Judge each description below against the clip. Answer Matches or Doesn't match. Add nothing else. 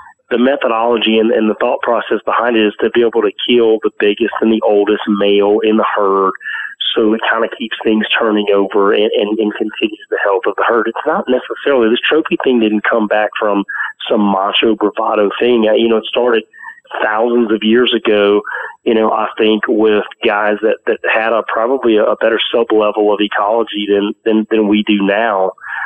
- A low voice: Matches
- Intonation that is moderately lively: Doesn't match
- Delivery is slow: Doesn't match